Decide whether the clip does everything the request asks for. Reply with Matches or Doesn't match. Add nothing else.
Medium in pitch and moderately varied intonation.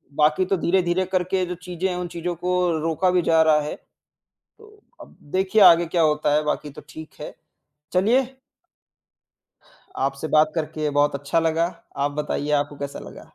Matches